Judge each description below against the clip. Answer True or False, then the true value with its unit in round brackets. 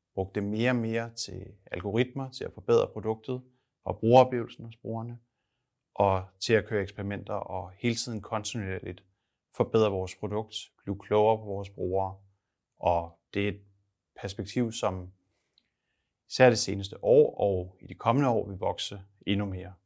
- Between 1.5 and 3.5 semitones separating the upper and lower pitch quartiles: True (3.1 semitones)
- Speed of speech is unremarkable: True (155 wpm)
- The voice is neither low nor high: False (105 Hz)